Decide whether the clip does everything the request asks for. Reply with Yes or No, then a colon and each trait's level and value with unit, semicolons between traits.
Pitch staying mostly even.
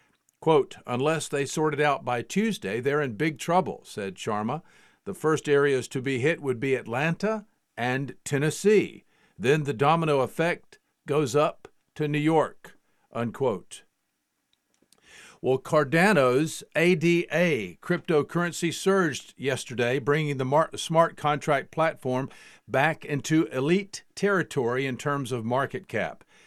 No: average, 3.6 semitones